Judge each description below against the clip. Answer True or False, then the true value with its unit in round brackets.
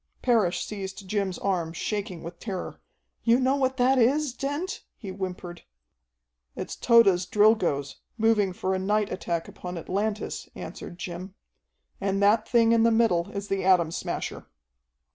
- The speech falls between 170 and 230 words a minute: False (145 wpm)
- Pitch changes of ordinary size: True (4.0 semitones)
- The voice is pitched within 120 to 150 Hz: False (200 Hz)